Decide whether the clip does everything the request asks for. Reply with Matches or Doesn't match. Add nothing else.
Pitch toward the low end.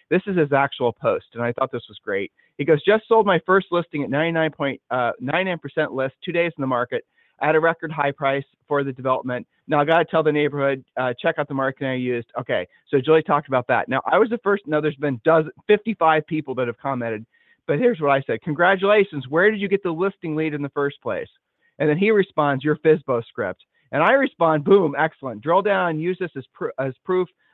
Doesn't match